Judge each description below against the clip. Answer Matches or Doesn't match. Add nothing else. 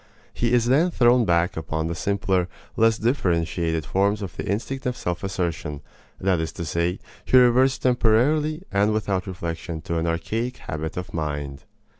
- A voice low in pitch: Matches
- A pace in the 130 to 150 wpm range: Doesn't match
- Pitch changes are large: Matches